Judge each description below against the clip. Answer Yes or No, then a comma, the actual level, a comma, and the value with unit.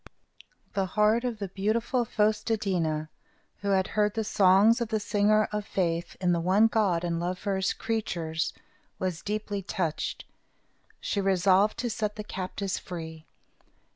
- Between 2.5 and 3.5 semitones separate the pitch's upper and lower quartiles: Yes, average, 2.9 semitones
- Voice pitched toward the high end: Yes, high, 200 Hz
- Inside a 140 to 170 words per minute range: Yes, average, 165 wpm